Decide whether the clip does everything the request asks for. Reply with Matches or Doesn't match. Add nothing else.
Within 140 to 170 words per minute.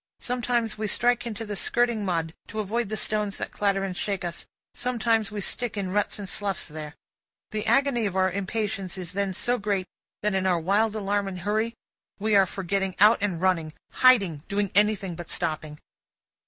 Doesn't match